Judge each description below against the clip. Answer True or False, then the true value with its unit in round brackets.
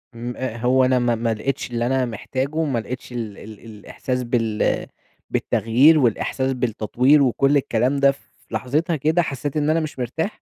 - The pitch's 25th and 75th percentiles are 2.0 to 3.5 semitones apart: True (3.1 semitones)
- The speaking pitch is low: True (130 Hz)